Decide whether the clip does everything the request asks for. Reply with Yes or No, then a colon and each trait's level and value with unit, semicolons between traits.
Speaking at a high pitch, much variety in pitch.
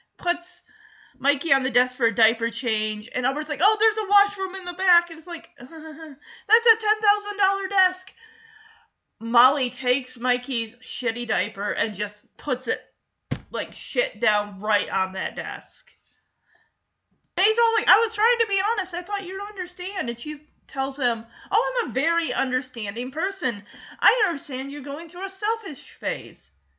Yes: very high, 310 Hz; wide, 8.6 semitones